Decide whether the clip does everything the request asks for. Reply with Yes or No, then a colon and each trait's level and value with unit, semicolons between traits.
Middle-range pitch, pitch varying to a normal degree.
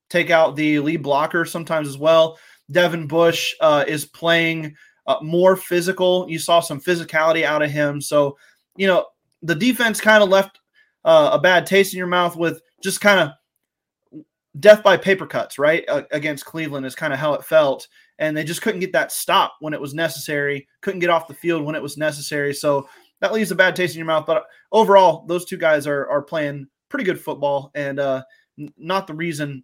Yes: medium, 165 Hz; average, 3.7 semitones